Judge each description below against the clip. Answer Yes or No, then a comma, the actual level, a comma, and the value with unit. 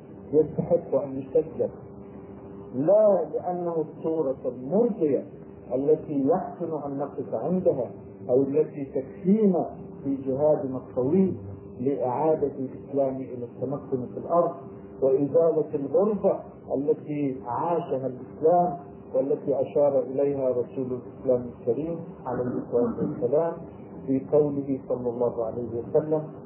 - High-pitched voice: No, medium, 140 Hz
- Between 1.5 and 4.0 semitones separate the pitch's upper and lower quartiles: No, average, 4.6 semitones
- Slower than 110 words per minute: Yes, average, 100 wpm